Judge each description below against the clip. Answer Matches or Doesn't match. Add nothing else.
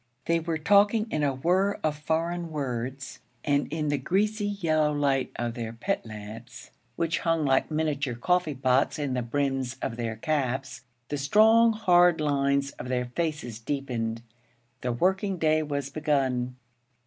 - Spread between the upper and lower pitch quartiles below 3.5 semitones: Doesn't match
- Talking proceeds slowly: Doesn't match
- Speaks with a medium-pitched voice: Matches